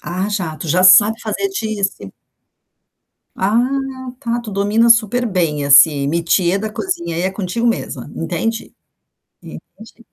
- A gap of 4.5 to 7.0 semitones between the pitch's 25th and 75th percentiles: Yes, average, 4.8 semitones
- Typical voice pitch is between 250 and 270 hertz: No, high, 200 Hz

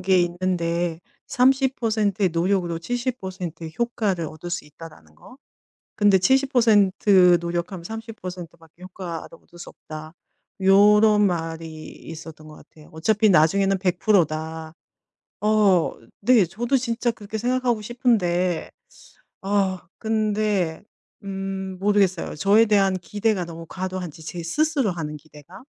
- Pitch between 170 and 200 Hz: Yes, high, 190 Hz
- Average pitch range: Yes, average, 4.1 semitones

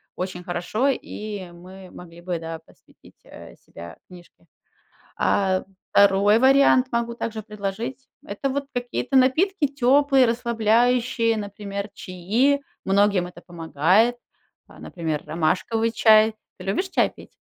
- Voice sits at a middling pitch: No, high, 210 Hz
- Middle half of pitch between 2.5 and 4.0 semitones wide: No, average, 5.1 semitones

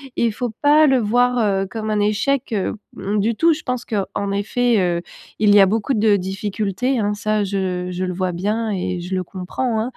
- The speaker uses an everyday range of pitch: Yes, average, 3.4 semitones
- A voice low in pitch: No, high, 210 Hz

